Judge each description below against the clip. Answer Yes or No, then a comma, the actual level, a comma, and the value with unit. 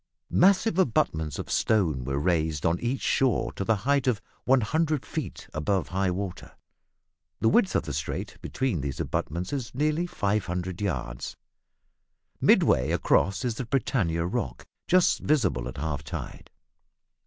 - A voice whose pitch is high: No, very low, 95 Hz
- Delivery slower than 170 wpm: Yes, average, 140 wpm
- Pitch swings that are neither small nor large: No, wide, 8.8 semitones